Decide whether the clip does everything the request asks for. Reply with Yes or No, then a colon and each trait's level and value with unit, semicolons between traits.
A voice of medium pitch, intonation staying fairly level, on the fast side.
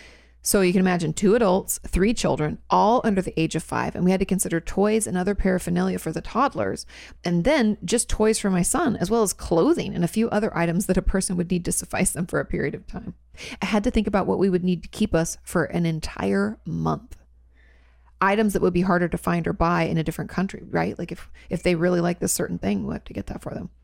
No: medium, 180 Hz; average, 3.3 semitones; fast, 255 wpm